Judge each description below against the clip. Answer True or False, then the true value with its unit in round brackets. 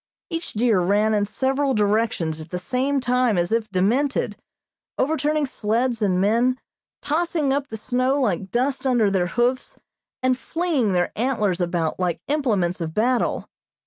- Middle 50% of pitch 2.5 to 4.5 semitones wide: False (5.2 semitones)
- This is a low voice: False (235 Hz)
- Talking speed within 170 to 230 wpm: False (150 wpm)